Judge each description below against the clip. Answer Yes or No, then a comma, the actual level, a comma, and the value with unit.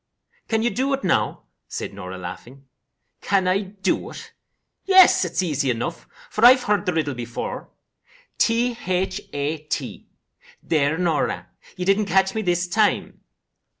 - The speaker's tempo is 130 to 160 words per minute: Yes, average, 145 wpm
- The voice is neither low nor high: Yes, medium, 180 Hz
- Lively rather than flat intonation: Yes, wide, 6.1 semitones